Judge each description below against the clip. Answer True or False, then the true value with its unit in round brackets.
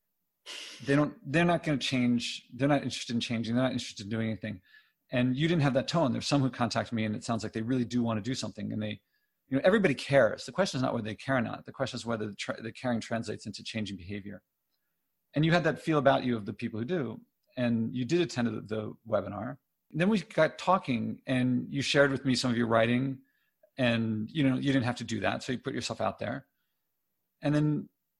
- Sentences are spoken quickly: True (250 wpm)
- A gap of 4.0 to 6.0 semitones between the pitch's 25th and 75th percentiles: False (3.5 semitones)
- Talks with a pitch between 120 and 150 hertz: True (125 Hz)